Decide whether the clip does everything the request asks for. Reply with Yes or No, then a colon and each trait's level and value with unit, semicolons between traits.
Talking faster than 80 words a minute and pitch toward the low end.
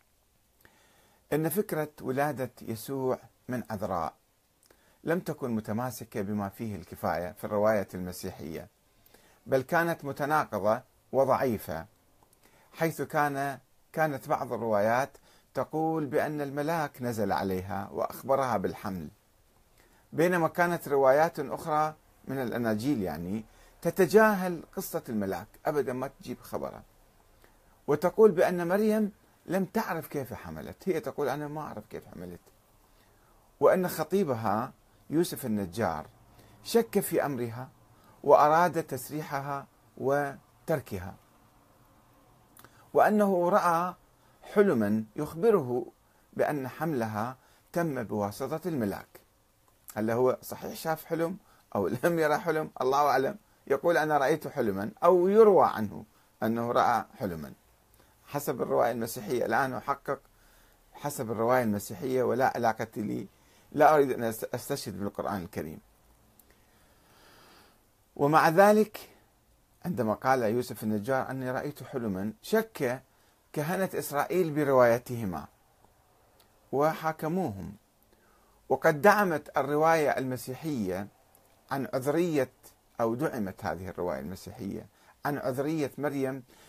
Yes: average, 100 wpm; low, 130 Hz